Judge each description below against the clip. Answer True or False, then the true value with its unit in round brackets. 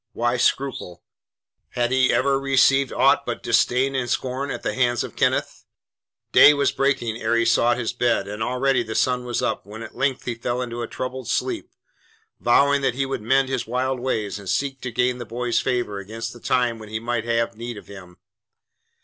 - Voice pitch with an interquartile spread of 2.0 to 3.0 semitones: True (2.4 semitones)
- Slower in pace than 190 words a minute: False (200 wpm)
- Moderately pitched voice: False (120 Hz)